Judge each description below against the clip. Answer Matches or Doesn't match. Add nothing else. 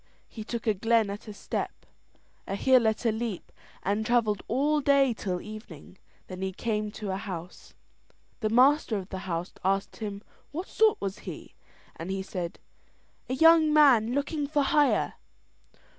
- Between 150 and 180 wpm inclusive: Matches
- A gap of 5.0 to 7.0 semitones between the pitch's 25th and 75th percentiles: Matches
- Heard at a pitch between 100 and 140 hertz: Doesn't match